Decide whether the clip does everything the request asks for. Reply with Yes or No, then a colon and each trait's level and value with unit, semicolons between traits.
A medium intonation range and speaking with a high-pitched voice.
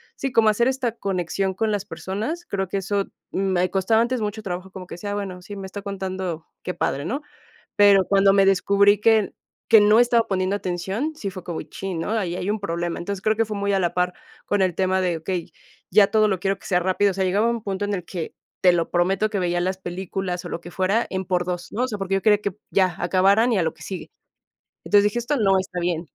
No: narrow, 2.3 semitones; high, 195 Hz